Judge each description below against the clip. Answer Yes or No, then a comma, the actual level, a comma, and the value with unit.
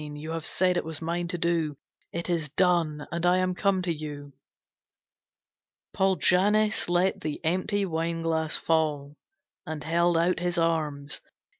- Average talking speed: Yes, average, 155 wpm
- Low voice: No, medium, 165 Hz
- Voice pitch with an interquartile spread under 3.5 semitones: Yes, narrow, 2.4 semitones